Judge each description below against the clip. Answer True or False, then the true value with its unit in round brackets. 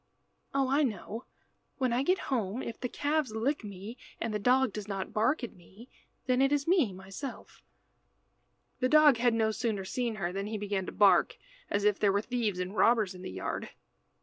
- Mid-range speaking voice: False (225 Hz)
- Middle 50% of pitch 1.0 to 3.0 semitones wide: False (4.3 semitones)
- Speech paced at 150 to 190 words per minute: False (200 wpm)